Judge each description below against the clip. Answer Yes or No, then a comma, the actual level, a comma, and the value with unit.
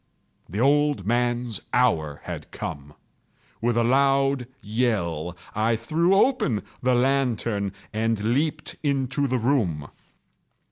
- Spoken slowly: Yes, slow, 110 wpm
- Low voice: Yes, low, 120 Hz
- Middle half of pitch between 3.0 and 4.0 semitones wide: No, average, 4.5 semitones